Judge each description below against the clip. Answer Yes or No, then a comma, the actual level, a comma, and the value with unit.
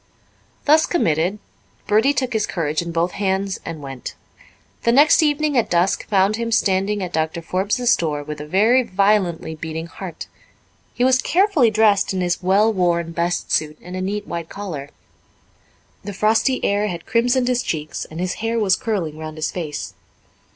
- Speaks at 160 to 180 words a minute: Yes, average, 170 wpm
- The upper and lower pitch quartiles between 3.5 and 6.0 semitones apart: Yes, average, 5.1 semitones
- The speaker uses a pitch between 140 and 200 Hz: Yes, high, 190 Hz